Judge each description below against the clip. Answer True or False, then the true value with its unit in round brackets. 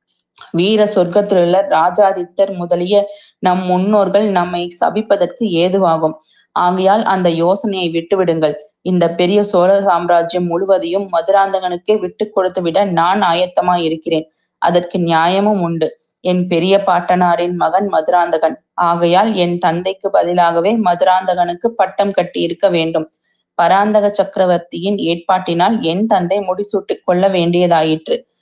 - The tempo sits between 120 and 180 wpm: False (105 wpm)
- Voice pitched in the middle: True (180 Hz)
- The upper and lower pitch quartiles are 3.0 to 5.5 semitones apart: False (2.5 semitones)